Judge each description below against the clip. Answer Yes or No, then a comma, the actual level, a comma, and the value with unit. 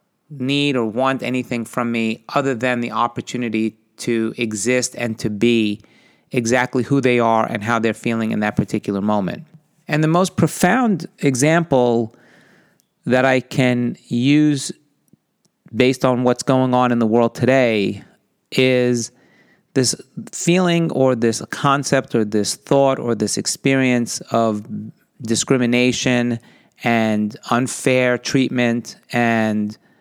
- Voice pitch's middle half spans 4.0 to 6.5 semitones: No, average, 2.7 semitones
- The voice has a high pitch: No, low, 125 Hz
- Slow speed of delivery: Yes, slow, 125 wpm